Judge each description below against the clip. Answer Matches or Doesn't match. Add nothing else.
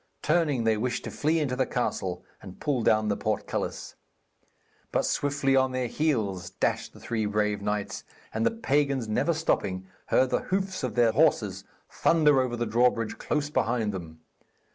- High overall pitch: Doesn't match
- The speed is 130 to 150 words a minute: Doesn't match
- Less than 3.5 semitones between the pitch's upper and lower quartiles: Doesn't match